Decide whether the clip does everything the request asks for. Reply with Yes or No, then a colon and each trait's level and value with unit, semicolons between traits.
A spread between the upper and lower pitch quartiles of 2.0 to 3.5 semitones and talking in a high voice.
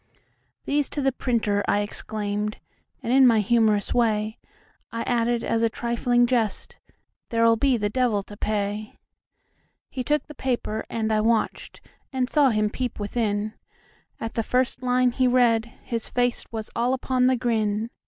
Yes: average, 2.7 semitones; high, 230 Hz